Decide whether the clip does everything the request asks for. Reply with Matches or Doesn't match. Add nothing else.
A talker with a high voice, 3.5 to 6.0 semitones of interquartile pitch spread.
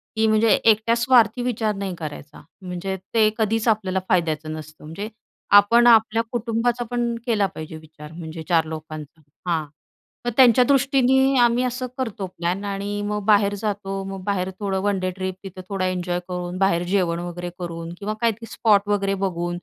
Matches